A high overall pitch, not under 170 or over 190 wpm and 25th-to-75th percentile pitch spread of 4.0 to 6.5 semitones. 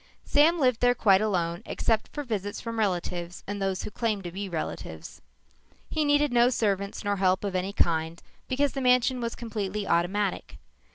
Yes: high, 205 Hz; average, 175 wpm; average, 4.5 semitones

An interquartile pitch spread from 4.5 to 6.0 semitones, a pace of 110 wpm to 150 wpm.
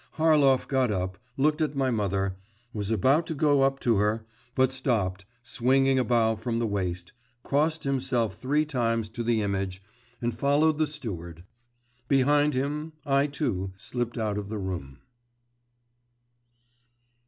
Yes: average, 5.2 semitones; average, 145 wpm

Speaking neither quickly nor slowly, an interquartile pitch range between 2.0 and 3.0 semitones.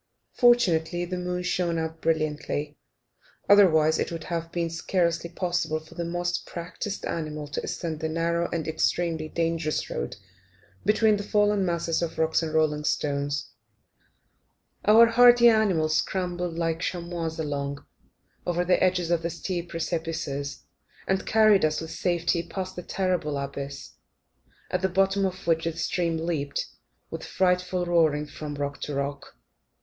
Yes: average, 150 wpm; narrow, 2.4 semitones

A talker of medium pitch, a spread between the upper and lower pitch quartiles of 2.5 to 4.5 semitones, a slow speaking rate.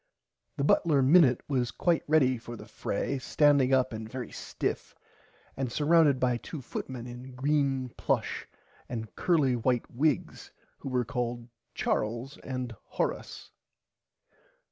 No: low, 130 Hz; average, 2.8 semitones; slow, 125 wpm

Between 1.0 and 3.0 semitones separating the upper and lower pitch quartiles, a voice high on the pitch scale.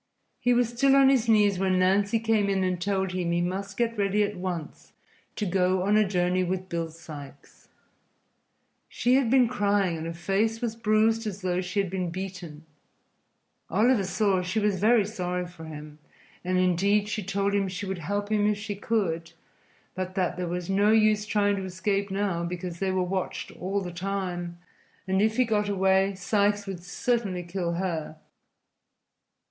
Yes: average, 2.7 semitones; high, 195 Hz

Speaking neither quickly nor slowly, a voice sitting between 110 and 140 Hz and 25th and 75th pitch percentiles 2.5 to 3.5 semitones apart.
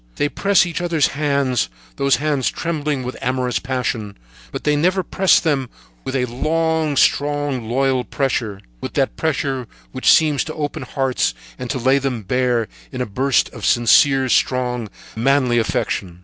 Yes: average, 160 wpm; low, 135 Hz; average, 2.8 semitones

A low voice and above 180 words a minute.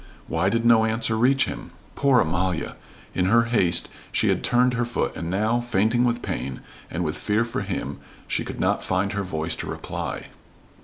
Yes: low, 110 Hz; average, 190 wpm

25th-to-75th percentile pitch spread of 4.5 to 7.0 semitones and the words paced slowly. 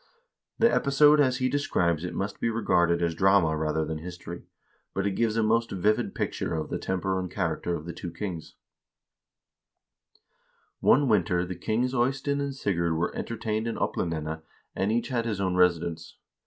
No: average, 5.3 semitones; average, 180 wpm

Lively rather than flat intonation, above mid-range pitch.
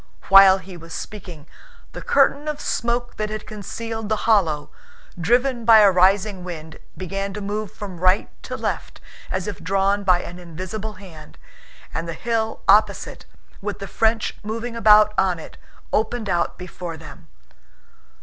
No: average, 3.3 semitones; high, 200 Hz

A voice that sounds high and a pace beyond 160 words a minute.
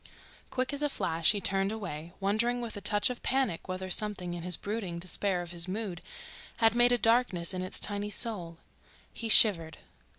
Yes: high, 200 Hz; average, 190 wpm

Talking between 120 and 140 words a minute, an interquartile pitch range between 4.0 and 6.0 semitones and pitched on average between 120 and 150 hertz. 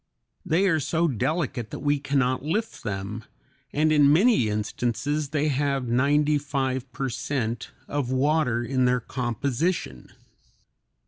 No: slow, 135 wpm; average, 3.6 semitones; medium, 140 Hz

